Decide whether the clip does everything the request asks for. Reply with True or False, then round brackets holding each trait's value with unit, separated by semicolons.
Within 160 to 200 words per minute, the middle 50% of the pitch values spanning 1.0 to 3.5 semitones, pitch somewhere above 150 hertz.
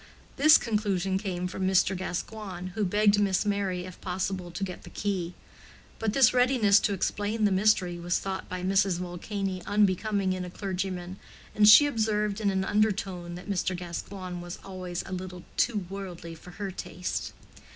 True (170 wpm; 2.4 semitones; 190 Hz)